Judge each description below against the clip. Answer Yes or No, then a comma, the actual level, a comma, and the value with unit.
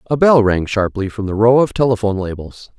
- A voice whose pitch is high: No, low, 110 Hz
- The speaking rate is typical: No, fast, 215 wpm